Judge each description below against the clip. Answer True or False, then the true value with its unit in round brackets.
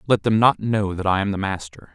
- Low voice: True (100 Hz)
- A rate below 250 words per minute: False (280 wpm)